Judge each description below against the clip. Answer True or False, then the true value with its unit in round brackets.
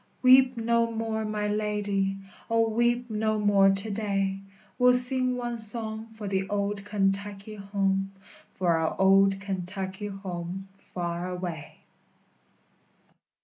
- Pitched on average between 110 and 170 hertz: False (205 Hz)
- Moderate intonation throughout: False (2.3 semitones)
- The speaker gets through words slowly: True (120 wpm)